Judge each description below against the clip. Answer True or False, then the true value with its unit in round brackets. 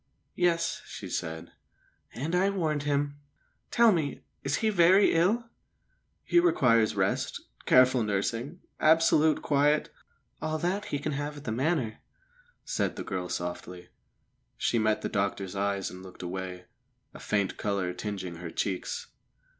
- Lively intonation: True (8.4 semitones)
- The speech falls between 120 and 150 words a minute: True (145 wpm)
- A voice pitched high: False (135 Hz)